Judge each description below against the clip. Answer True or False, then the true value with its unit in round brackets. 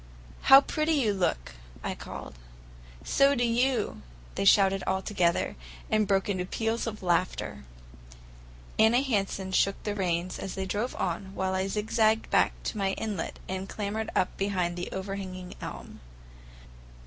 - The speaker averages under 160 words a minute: True (145 wpm)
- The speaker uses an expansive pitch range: False (2.8 semitones)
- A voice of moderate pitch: False (195 Hz)